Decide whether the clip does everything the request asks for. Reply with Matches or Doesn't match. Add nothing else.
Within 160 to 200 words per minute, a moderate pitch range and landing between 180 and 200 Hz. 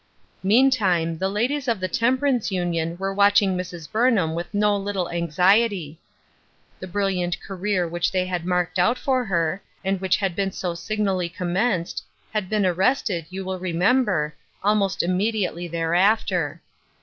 Doesn't match